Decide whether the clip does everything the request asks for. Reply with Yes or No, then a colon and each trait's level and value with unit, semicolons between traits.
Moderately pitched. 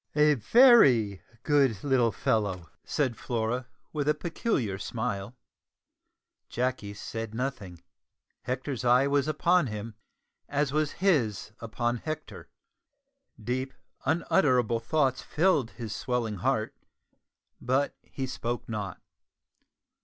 No: low, 125 Hz